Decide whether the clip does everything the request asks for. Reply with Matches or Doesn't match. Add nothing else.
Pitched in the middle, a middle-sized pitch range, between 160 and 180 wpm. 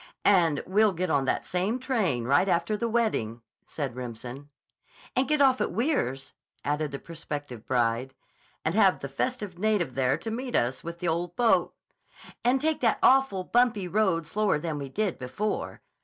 Doesn't match